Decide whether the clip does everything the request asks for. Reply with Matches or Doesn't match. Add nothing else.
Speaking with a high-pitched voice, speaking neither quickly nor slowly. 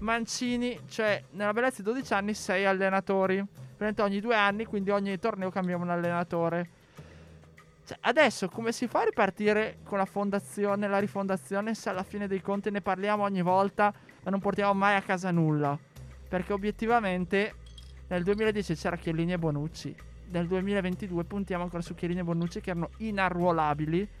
Matches